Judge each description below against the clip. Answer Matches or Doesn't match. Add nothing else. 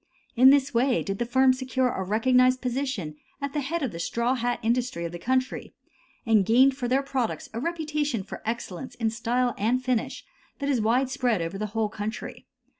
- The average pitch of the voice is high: Matches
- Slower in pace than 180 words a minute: Doesn't match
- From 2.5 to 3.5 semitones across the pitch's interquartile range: Matches